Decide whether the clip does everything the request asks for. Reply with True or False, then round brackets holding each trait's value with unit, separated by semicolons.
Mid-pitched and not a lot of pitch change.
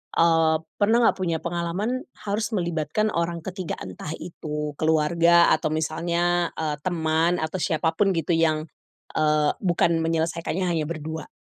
True (165 Hz; 1.8 semitones)